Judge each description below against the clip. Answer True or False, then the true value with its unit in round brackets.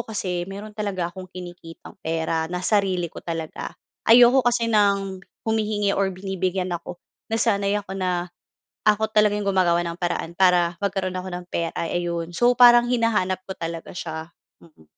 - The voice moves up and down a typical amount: True (3.1 semitones)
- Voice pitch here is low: False (185 Hz)